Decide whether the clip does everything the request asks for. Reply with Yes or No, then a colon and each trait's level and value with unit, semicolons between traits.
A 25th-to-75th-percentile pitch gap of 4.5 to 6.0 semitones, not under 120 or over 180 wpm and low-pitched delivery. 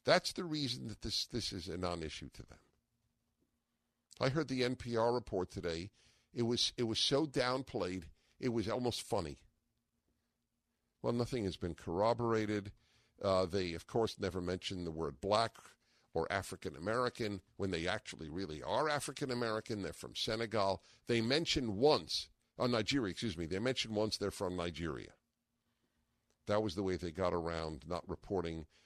Yes: average, 5.0 semitones; average, 160 wpm; low, 105 Hz